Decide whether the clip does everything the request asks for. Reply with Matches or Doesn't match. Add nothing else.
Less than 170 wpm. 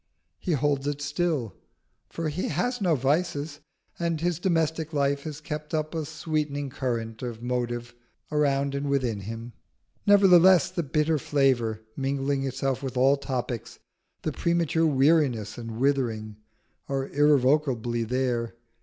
Matches